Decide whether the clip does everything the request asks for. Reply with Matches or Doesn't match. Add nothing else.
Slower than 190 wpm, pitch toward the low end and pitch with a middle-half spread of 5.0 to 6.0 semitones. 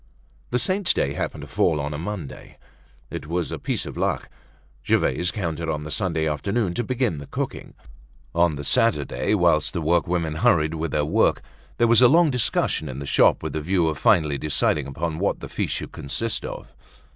Doesn't match